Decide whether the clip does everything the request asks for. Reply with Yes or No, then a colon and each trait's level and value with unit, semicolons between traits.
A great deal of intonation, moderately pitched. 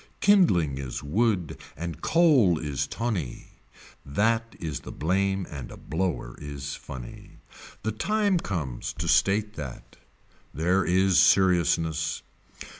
No: wide, 5.8 semitones; very low, 90 Hz